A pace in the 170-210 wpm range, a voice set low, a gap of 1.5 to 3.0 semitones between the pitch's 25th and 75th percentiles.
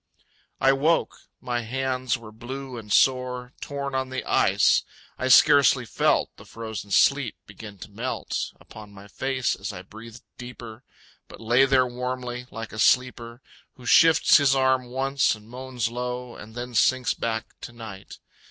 No: average, 160 wpm; low, 125 Hz; narrow, 2.6 semitones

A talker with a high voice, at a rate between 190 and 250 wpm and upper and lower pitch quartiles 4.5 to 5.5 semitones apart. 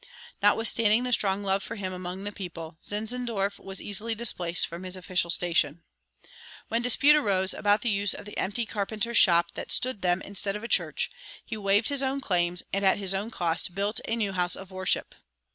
No: high, 200 Hz; average, 195 wpm; average, 3.3 semitones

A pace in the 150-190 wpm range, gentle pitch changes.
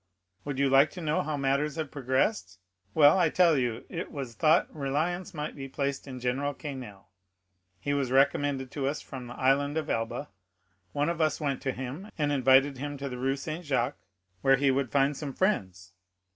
No: average, 200 wpm; narrow, 2.2 semitones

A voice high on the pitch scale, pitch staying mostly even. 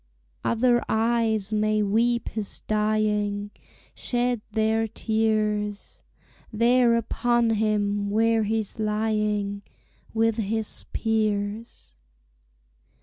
Yes: high, 220 Hz; narrow, 1.4 semitones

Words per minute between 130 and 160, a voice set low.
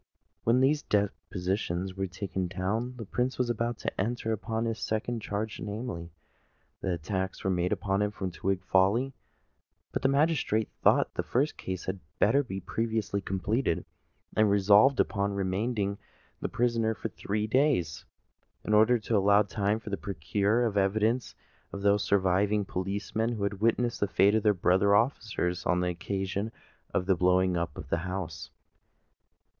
Yes: average, 155 wpm; low, 100 Hz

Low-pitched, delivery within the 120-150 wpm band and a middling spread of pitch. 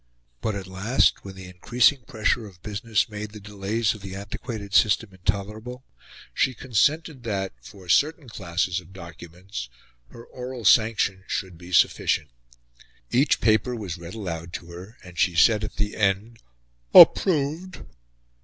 Yes: low, 105 Hz; average, 145 wpm; average, 3.9 semitones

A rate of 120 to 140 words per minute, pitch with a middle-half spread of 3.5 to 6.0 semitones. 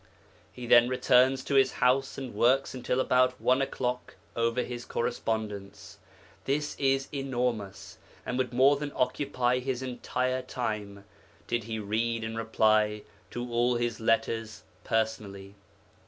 No: slow, 135 wpm; narrow, 2.5 semitones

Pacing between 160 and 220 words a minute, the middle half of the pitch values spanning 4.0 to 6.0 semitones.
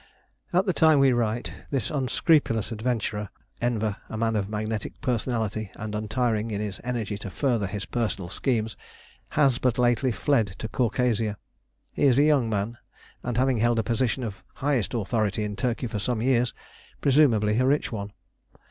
No: average, 165 wpm; average, 3.1 semitones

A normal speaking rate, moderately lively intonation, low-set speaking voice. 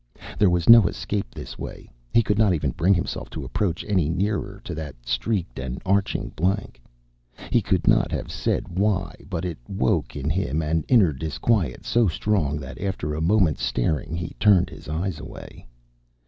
Yes: average, 175 wpm; average, 4.7 semitones; very low, 90 Hz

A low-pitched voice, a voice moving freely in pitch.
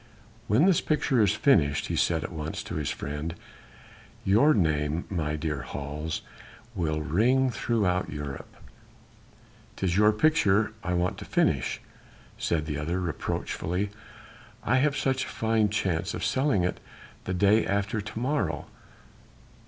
Yes: very low, 95 Hz; wide, 6.1 semitones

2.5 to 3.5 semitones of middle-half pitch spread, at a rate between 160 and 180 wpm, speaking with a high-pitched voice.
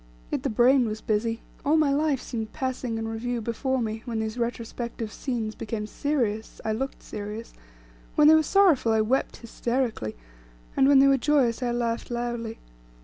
Yes: average, 3.1 semitones; average, 170 wpm; high, 235 Hz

